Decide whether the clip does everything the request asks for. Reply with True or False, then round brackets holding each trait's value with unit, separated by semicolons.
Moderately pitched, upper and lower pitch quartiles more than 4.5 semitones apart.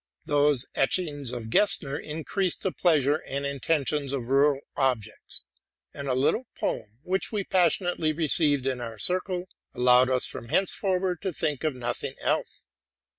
True (145 Hz; 5.3 semitones)